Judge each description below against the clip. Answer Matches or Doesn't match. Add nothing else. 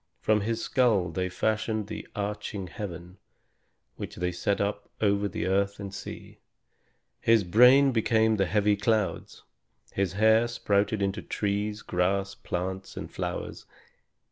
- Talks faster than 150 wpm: Doesn't match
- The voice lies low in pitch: Matches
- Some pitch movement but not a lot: Doesn't match